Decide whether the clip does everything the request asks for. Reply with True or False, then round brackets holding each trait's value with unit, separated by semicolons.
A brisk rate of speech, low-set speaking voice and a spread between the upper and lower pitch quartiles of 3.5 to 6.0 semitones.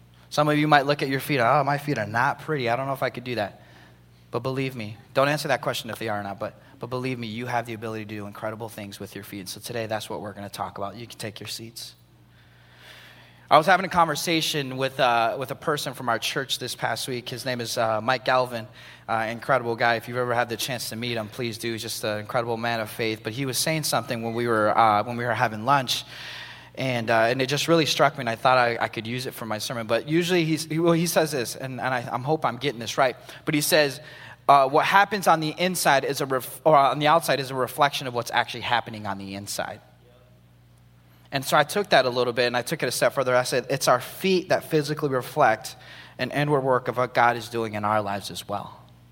True (265 wpm; 120 Hz; 4.2 semitones)